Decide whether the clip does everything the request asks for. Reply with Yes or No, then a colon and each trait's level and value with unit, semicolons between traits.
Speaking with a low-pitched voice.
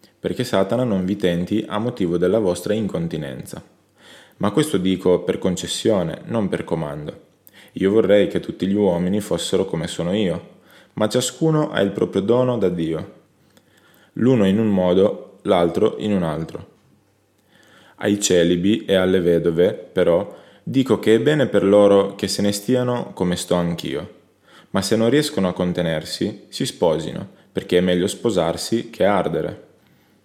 Yes: low, 100 Hz